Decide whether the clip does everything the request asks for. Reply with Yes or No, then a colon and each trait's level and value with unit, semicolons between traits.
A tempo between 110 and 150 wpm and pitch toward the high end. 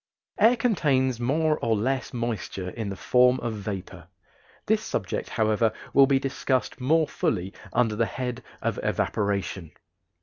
No: average, 140 wpm; low, 120 Hz